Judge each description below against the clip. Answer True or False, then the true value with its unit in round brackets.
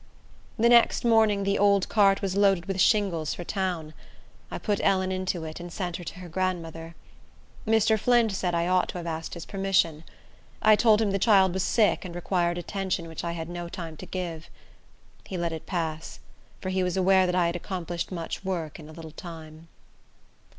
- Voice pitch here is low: False (180 Hz)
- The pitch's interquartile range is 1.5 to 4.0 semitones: True (2.7 semitones)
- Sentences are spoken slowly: False (200 wpm)